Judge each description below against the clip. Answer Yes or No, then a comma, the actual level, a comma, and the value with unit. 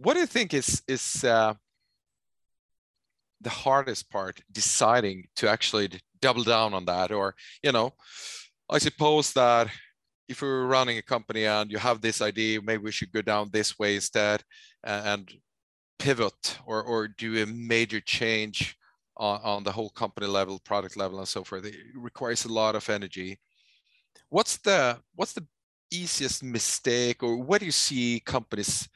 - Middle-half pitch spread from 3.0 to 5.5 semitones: Yes, average, 3.6 semitones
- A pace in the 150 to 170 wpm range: Yes, average, 160 wpm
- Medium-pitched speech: No, low, 110 Hz